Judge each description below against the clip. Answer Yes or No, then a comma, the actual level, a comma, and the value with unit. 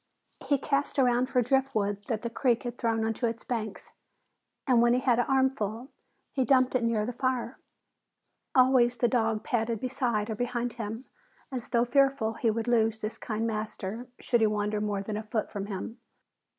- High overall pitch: Yes, high, 235 Hz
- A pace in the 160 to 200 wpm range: Yes, average, 185 wpm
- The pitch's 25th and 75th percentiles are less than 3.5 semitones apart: Yes, narrow, 2.5 semitones